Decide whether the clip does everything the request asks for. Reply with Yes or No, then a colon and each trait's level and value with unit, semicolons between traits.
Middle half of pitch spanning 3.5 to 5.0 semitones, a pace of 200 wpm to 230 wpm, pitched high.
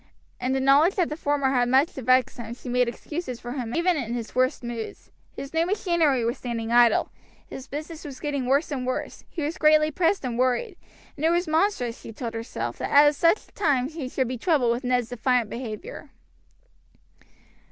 Yes: average, 4.2 semitones; fast, 205 wpm; very high, 265 Hz